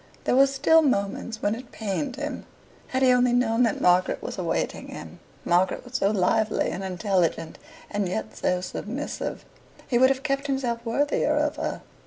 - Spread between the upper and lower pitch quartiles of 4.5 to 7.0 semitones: Yes, wide, 5.4 semitones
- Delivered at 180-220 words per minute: No, average, 170 wpm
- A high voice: Yes, high, 235 Hz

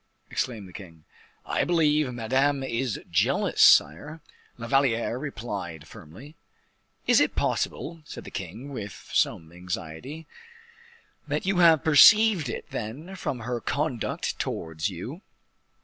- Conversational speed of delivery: No, slow, 125 wpm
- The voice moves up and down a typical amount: No, wide, 7.6 semitones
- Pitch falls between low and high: No, low, 125 Hz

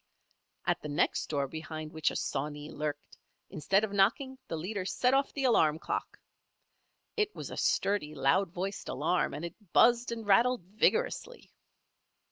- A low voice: No, high, 190 Hz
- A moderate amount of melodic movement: No, wide, 7.3 semitones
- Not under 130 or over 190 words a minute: Yes, average, 155 wpm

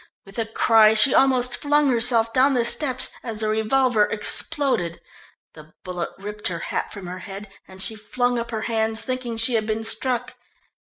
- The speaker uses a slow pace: No, average, 180 wpm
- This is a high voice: Yes, high, 225 Hz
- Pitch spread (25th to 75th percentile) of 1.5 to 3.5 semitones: Yes, average, 3.0 semitones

